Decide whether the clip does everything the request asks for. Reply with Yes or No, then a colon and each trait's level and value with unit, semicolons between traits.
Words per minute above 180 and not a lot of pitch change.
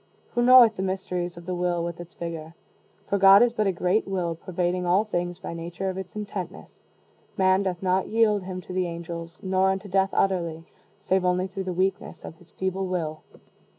Yes: average, 200 wpm; narrow, 1.8 semitones